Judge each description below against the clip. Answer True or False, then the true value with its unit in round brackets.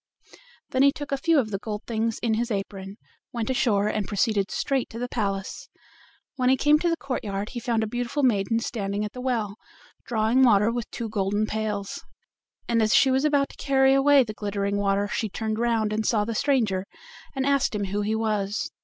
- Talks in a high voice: True (220 Hz)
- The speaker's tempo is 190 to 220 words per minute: True (205 wpm)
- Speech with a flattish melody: False (3.9 semitones)